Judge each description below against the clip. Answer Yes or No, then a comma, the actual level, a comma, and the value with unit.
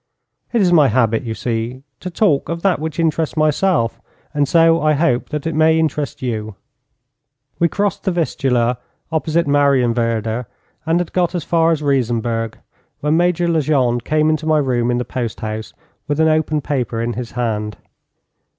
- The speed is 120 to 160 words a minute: No, average, 170 wpm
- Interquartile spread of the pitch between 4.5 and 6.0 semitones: Yes, average, 5.2 semitones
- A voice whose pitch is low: No, medium, 145 Hz